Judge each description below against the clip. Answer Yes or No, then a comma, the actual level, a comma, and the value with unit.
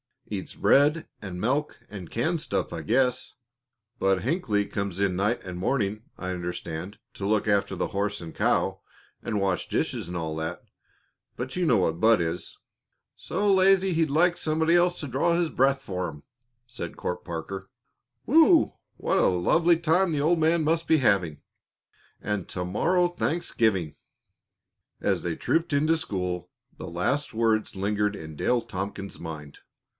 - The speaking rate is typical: Yes, average, 160 wpm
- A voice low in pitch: Yes, low, 105 Hz